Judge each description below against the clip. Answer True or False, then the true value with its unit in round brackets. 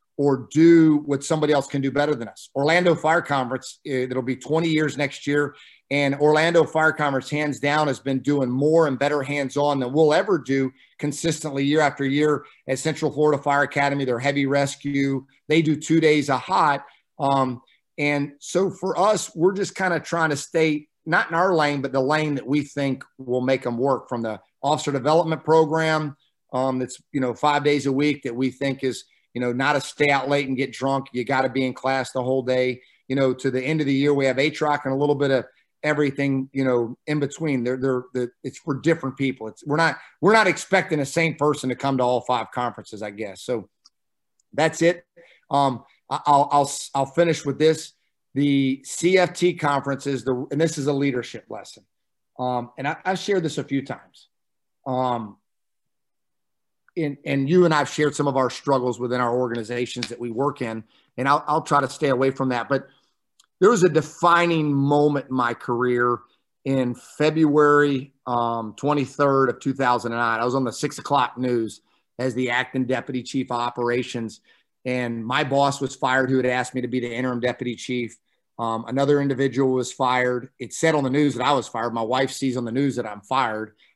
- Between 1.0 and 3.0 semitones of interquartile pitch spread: True (2.7 semitones)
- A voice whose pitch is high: False (140 Hz)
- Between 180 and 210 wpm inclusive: True (205 wpm)